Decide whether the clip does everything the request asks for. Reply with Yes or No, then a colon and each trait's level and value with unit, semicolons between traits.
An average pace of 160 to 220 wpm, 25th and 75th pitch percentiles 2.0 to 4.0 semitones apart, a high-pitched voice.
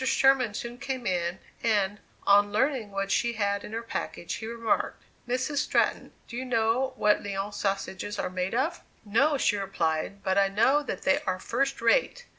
No: average, 180 wpm; average, 4.6 semitones; high, 220 Hz